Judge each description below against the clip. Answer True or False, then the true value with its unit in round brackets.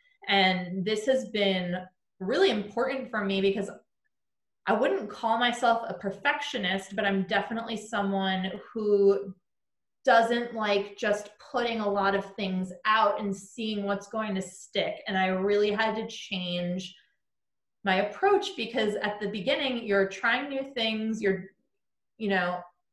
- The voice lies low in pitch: False (205 Hz)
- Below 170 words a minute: True (140 wpm)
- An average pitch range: True (3.0 semitones)